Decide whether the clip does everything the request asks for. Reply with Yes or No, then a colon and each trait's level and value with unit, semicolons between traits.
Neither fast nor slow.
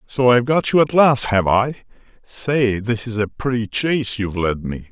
No: fast, 210 wpm